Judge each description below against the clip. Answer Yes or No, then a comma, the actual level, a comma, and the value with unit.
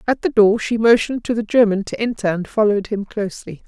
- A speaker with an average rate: No, fast, 230 wpm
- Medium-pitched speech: No, high, 215 Hz